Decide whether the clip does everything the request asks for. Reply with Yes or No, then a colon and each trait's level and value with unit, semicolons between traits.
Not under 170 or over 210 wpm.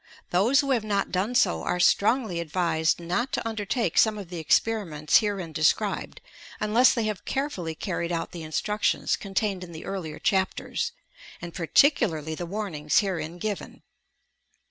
No: average, 155 wpm